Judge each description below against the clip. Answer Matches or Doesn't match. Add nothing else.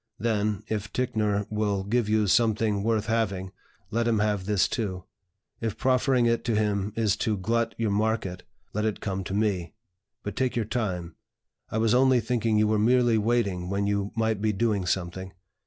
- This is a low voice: Matches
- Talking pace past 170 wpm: Matches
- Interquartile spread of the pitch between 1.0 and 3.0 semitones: Matches